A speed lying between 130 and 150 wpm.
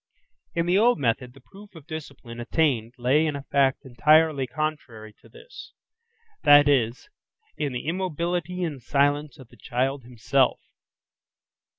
Yes: average, 145 wpm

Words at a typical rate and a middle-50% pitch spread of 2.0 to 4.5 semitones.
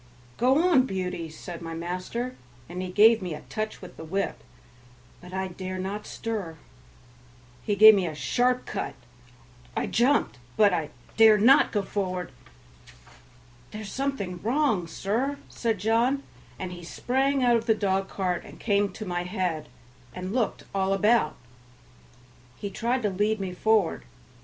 Yes: average, 155 wpm; average, 4.1 semitones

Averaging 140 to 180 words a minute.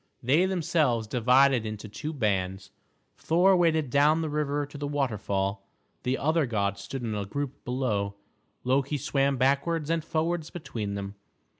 Yes: average, 150 wpm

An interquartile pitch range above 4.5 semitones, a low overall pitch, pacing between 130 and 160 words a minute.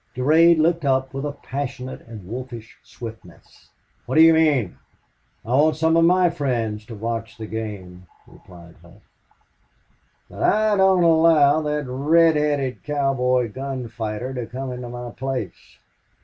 Yes: average, 5.2 semitones; low, 130 Hz; average, 150 wpm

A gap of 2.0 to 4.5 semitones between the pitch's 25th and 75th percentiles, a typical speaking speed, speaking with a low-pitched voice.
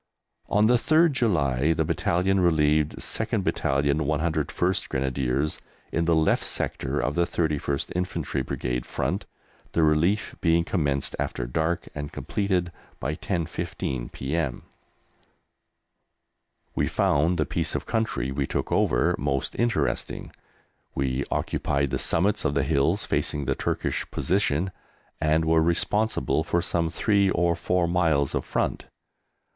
No: average, 4.0 semitones; slow, 130 wpm; very low, 80 Hz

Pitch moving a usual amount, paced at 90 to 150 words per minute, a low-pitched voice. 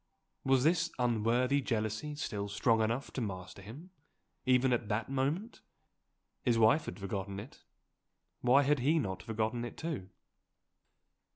Yes: average, 4.3 semitones; slow, 135 wpm; low, 120 Hz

